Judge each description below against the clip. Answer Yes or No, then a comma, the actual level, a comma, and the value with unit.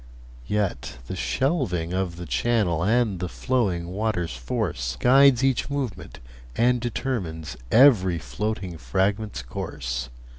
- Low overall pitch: Yes, very low, 95 Hz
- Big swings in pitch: Yes, wide, 6.1 semitones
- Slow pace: Yes, slow, 115 wpm